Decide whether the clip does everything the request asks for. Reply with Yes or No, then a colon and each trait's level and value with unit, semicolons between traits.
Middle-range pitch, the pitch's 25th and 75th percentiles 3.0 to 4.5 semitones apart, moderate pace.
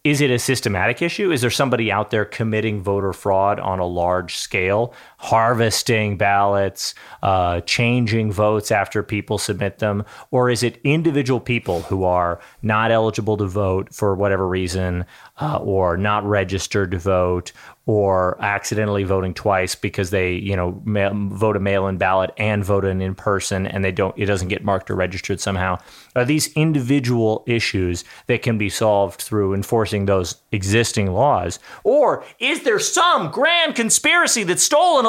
No: low, 105 Hz; average, 3.4 semitones; average, 160 wpm